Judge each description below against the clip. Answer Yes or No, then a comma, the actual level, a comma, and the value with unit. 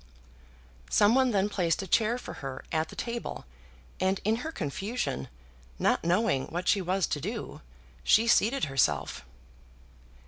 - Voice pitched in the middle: No, high, 195 Hz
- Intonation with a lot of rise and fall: Yes, wide, 6.3 semitones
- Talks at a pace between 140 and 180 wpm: Yes, average, 145 wpm